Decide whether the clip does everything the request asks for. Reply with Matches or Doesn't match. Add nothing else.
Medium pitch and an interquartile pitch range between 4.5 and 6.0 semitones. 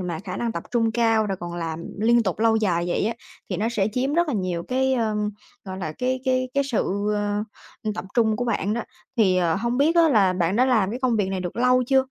Doesn't match